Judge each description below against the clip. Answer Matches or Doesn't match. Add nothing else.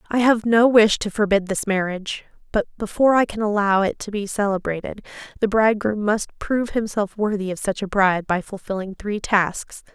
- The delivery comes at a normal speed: Matches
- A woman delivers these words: Matches